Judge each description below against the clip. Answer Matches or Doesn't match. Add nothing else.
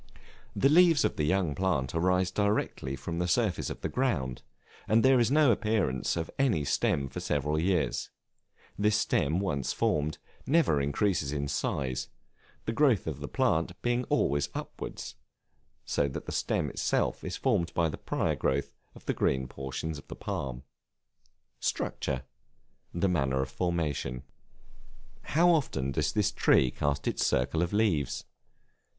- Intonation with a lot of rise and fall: Matches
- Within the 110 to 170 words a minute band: Matches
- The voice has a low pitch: Matches